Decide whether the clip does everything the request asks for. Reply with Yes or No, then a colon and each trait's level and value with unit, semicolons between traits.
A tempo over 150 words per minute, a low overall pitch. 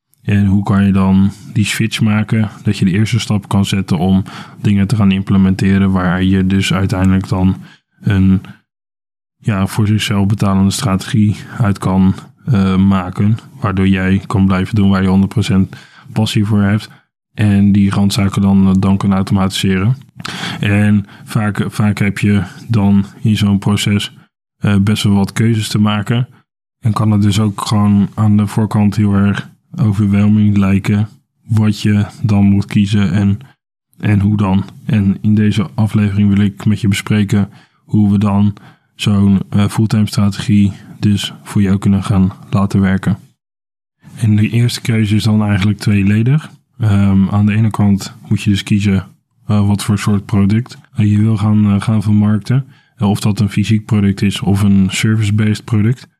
Yes: average, 165 wpm; low, 105 Hz